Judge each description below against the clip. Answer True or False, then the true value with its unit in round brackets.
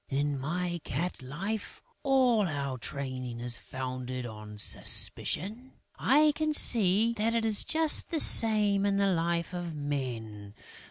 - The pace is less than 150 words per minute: True (140 wpm)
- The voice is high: False (170 Hz)